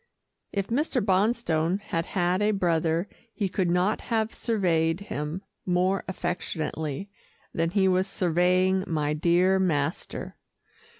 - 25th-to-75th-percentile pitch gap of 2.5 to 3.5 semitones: Yes, average, 2.9 semitones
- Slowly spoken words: Yes, slow, 120 wpm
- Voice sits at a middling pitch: Yes, medium, 180 Hz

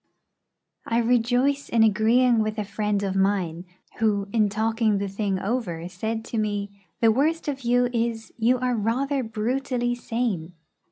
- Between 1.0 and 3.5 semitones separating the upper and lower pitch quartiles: Yes, average, 3.1 semitones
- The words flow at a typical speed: Yes, average, 155 wpm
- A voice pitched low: No, high, 225 Hz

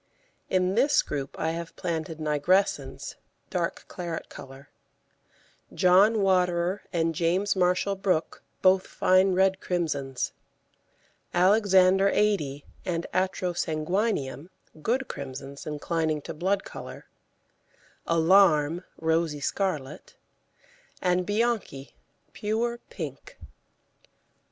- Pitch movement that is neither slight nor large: Yes, average, 3.7 semitones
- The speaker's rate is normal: No, slow, 90 wpm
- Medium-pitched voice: Yes, medium, 180 Hz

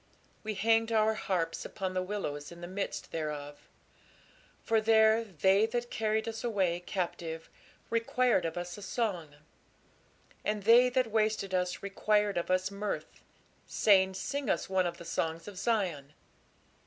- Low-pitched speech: No, high, 200 Hz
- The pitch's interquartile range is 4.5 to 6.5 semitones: No, average, 3.9 semitones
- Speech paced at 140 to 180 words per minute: Yes, average, 150 wpm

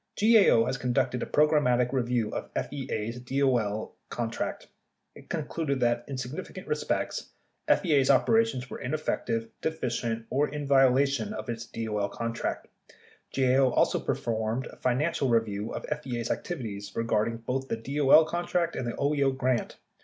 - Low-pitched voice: Yes, low, 130 Hz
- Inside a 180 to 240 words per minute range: No, average, 145 wpm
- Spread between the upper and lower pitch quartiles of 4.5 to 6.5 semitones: No, average, 3.5 semitones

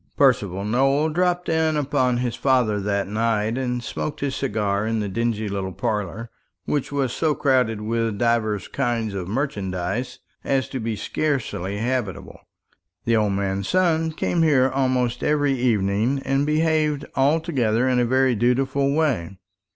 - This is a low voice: Yes, low, 125 Hz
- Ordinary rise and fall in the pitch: Yes, average, 4.7 semitones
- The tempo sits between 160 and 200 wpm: No, average, 150 wpm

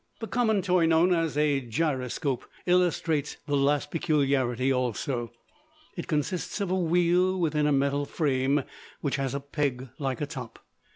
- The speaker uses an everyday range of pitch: Yes, average, 3.8 semitones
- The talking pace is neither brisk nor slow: Yes, average, 155 wpm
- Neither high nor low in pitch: Yes, medium, 145 Hz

